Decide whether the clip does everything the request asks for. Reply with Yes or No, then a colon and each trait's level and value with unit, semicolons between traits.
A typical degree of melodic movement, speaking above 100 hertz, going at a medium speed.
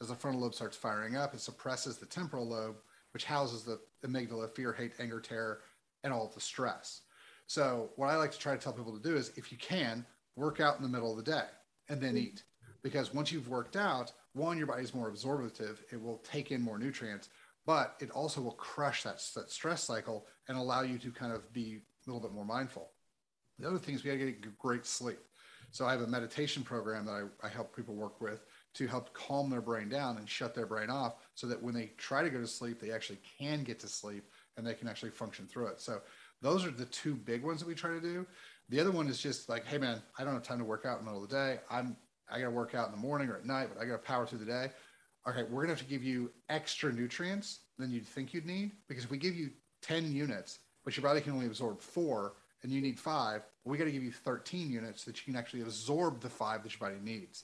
No: average, 3.5 semitones; low, 125 Hz; fast, 260 wpm